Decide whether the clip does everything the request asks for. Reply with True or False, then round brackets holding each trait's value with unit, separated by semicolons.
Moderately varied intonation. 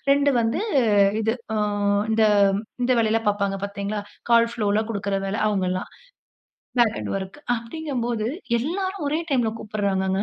True (3.3 semitones)